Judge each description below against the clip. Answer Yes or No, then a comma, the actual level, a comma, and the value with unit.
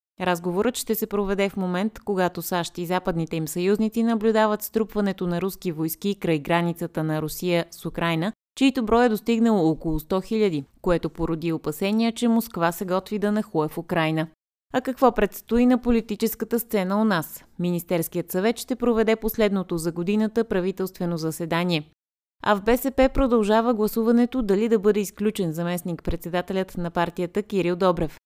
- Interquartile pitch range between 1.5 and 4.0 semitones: No, average, 4.4 semitones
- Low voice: No, high, 195 Hz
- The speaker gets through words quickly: No, average, 155 wpm